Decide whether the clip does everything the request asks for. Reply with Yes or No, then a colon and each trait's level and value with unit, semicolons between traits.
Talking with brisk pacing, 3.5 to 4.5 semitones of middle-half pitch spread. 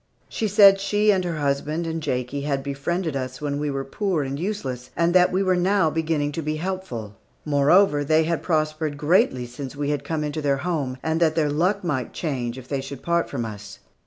Yes: fast, 220 wpm; average, 3.8 semitones